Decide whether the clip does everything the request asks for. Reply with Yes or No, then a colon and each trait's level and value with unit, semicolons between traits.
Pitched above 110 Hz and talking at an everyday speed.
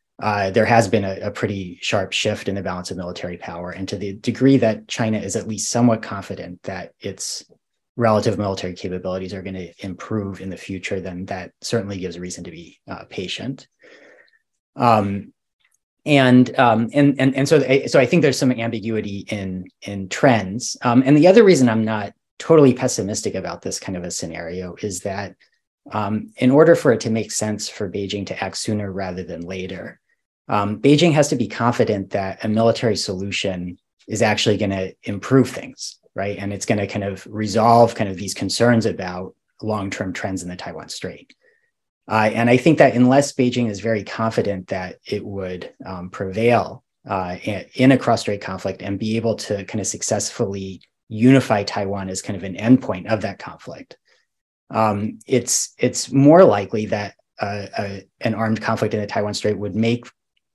No: low, 105 Hz; average, 185 wpm